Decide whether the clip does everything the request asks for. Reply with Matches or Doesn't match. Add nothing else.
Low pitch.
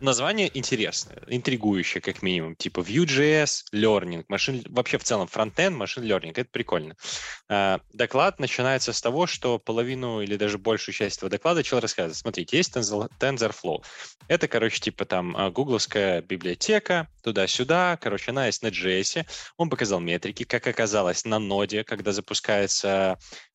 Matches